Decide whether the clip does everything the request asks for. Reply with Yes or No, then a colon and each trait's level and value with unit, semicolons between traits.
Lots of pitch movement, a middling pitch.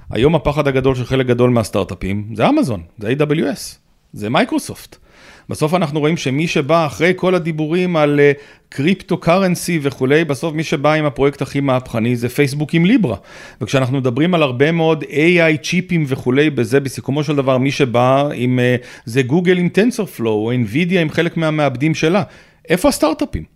No: average, 4.0 semitones; medium, 150 Hz